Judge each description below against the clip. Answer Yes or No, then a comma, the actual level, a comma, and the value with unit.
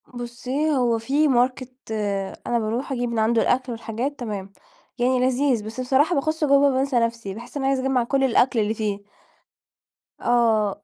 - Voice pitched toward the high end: Yes, high, 245 Hz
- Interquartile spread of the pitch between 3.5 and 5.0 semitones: No, average, 2.8 semitones